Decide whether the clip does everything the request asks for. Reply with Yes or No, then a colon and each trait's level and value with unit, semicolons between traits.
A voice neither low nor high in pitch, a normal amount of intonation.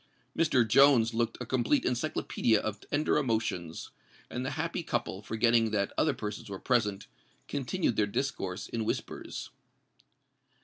No: low, 115 Hz; average, 4.4 semitones